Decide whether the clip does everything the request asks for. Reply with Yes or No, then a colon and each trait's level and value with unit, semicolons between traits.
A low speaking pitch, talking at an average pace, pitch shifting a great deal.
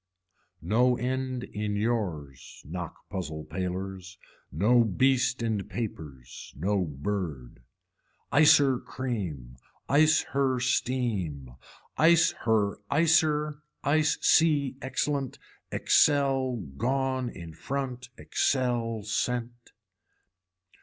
No: low, 120 Hz; slow, 85 wpm; wide, 6.3 semitones